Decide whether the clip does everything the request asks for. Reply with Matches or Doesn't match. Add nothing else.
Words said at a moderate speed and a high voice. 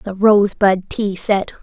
Matches